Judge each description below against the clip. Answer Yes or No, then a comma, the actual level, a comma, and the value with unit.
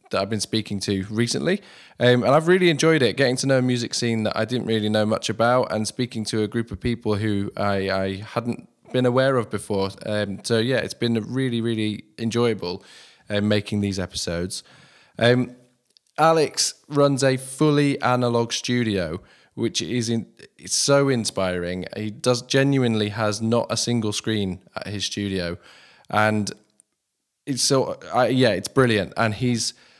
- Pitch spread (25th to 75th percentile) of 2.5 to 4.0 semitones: Yes, average, 3.2 semitones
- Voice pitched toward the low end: Yes, low, 115 Hz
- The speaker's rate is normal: Yes, average, 170 wpm